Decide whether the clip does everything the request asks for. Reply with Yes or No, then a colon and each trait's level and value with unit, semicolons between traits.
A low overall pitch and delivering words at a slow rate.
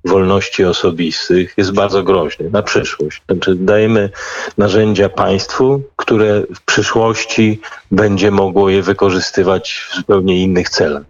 No: low, 100 Hz; average, 120 wpm